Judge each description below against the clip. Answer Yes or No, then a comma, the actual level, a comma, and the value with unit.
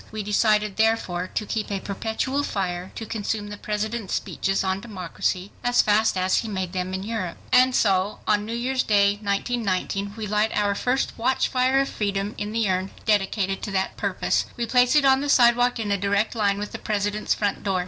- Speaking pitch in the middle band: No, high, 210 Hz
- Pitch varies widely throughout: No, narrow, 2.6 semitones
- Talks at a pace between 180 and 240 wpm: Yes, average, 200 wpm